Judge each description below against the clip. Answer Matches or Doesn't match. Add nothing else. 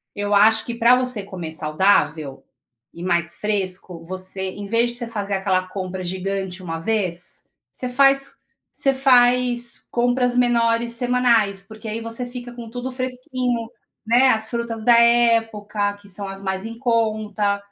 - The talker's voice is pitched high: Matches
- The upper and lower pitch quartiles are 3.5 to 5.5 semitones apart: Matches